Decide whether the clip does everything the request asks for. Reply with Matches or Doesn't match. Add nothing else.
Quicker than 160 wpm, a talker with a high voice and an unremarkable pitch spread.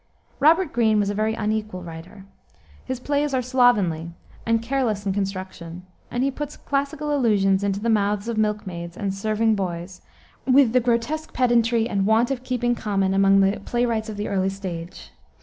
Matches